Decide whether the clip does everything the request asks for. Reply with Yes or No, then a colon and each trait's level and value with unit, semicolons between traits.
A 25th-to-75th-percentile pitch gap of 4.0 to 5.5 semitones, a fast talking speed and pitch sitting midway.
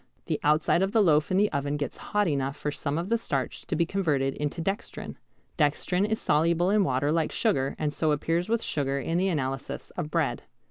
Yes: average, 4.4 semitones; fast, 215 wpm; medium, 155 Hz